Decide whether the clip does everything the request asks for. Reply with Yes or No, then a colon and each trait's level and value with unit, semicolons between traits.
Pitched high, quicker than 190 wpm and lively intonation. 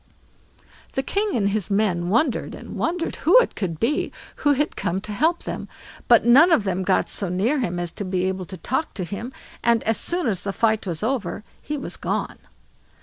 Yes: high, 215 Hz; fast, 205 wpm; wide, 6.5 semitones